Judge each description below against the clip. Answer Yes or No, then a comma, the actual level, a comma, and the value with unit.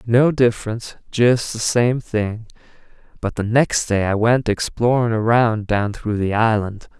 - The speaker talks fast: No, average, 155 wpm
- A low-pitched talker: Yes, low, 115 Hz